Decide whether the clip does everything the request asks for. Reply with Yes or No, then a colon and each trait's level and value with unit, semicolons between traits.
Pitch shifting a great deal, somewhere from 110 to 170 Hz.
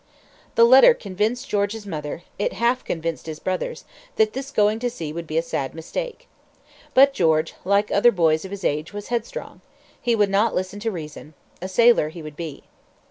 No: wide, 6.3 semitones; high, 200 Hz